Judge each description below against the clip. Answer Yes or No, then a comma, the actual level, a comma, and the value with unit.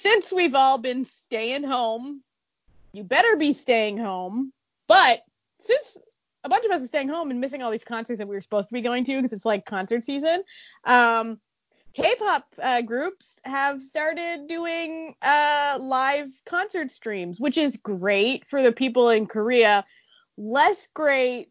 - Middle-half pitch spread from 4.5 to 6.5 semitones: Yes, wide, 5.4 semitones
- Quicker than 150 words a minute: Yes, average, 165 wpm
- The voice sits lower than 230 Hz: No, very high, 265 Hz